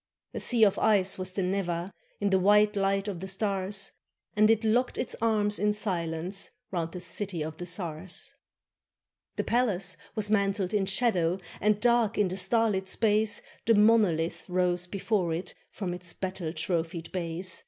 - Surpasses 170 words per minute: No, average, 165 wpm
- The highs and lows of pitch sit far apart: No, average, 3.0 semitones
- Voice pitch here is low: No, high, 195 Hz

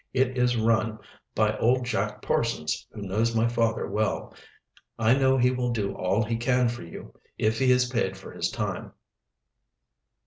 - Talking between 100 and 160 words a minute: No, average, 170 wpm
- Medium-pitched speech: No, low, 115 Hz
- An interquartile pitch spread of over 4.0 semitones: No, narrow, 2.4 semitones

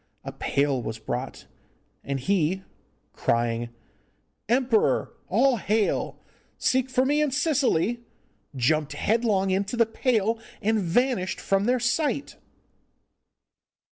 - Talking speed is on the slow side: Yes, slow, 105 wpm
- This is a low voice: No, high, 215 Hz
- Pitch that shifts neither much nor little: No, wide, 7.9 semitones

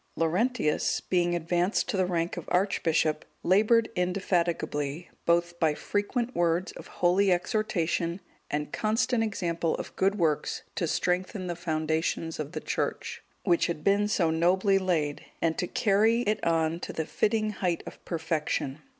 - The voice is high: No, medium, 175 Hz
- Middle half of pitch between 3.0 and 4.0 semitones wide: Yes, average, 3.4 semitones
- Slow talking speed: No, average, 150 wpm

